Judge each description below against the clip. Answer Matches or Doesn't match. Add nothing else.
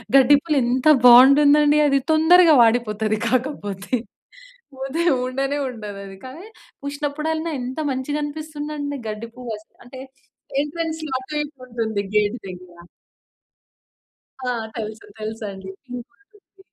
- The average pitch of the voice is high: Matches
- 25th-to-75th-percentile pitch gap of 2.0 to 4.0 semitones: Doesn't match